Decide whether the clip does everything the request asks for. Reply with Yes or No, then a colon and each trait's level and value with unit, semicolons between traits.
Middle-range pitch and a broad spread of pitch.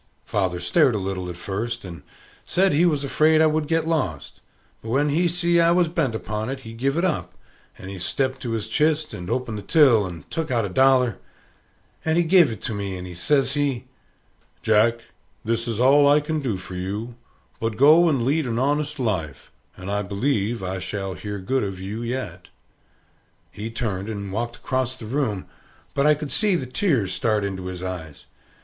No: low, 120 Hz; wide, 6.7 semitones